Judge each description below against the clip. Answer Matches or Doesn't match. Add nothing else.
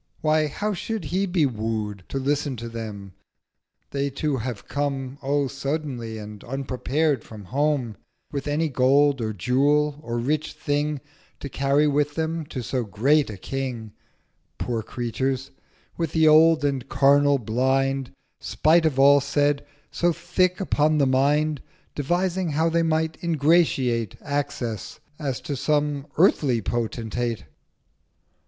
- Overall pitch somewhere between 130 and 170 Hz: Matches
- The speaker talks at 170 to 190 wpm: Doesn't match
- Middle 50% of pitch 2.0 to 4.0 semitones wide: Matches